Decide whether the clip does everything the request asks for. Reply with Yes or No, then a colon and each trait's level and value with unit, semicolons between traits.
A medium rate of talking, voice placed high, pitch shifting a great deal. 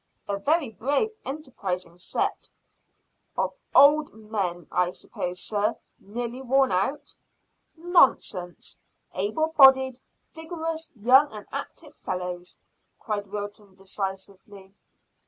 No: slow, 100 wpm; high, 215 Hz; wide, 6.5 semitones